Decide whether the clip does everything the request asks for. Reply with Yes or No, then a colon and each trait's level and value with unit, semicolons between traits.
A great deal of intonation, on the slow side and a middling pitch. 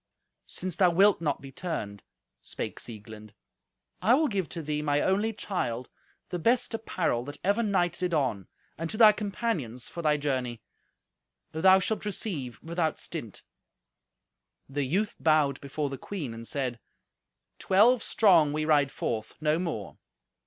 No: wide, 6.1 semitones; average, 150 wpm; medium, 160 Hz